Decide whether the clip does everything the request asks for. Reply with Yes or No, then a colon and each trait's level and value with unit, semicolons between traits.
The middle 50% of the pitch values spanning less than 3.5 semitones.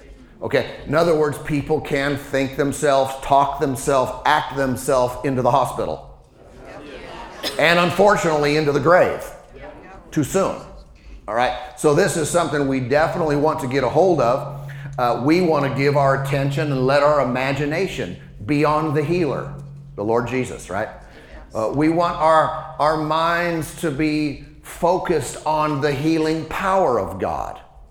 Yes: narrow, 2.5 semitones